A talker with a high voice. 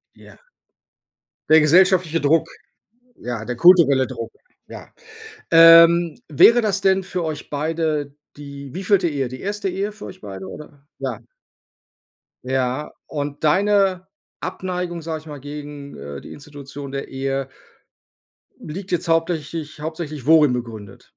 No: medium, 150 Hz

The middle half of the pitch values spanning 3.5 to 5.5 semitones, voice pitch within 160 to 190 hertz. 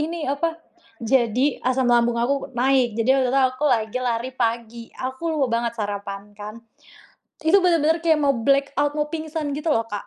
No: average, 4.2 semitones; very high, 255 Hz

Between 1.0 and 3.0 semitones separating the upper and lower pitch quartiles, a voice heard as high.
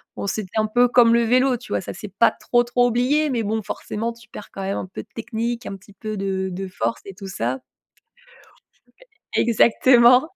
No: average, 3.6 semitones; high, 225 Hz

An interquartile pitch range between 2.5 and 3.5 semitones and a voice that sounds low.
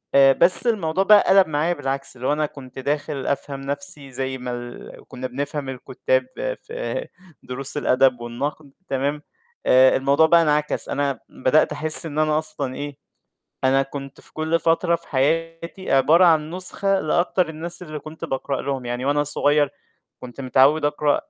No: average, 3.2 semitones; medium, 145 Hz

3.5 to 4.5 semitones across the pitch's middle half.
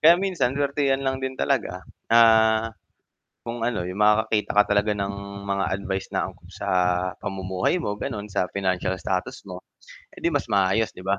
No: average, 5.1 semitones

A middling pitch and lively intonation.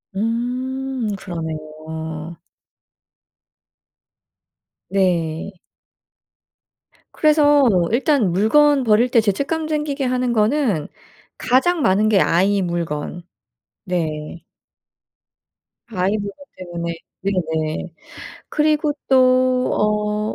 No: high, 210 Hz; wide, 7.1 semitones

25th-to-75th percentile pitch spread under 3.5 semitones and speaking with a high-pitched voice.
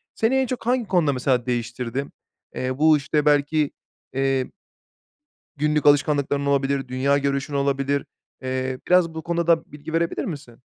No: average, 2.9 semitones; medium, 140 Hz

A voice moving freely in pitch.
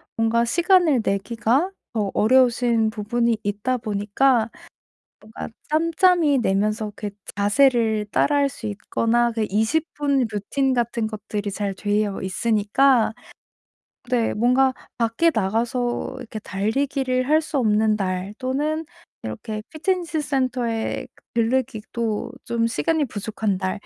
No: average, 3.8 semitones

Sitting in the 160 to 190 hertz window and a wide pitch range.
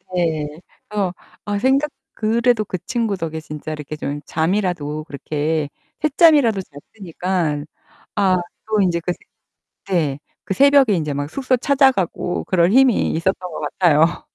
Yes: medium, 185 Hz; wide, 6.1 semitones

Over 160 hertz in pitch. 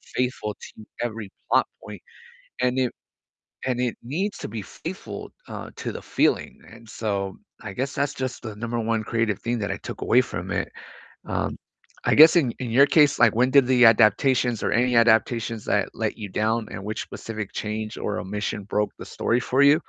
No: low, 115 Hz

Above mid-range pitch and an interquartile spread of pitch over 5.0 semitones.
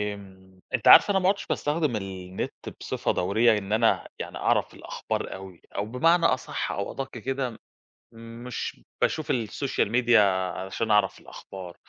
No: low, 110 Hz; wide, 5.5 semitones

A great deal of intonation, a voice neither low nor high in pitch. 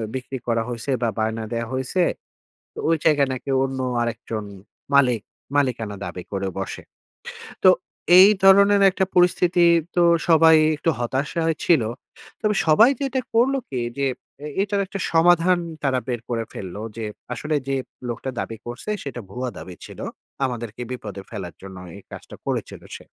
No: wide, 6.9 semitones; low, 130 Hz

